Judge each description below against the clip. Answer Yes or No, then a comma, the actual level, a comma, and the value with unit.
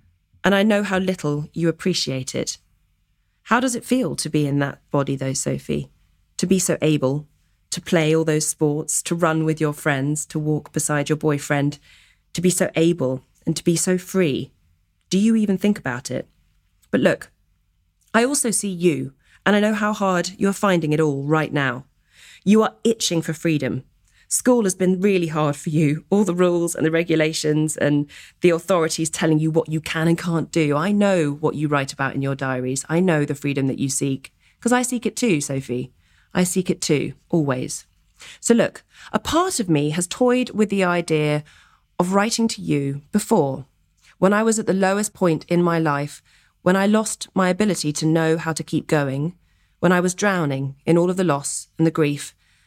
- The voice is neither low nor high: Yes, medium, 160 Hz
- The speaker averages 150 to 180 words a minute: No, average, 200 wpm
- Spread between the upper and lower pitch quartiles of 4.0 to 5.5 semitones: Yes, average, 4.6 semitones